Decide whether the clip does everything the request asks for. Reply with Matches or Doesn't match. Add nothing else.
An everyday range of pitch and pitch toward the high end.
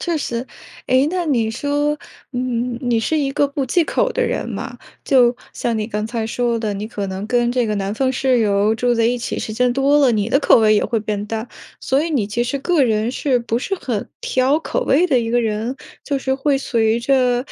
Matches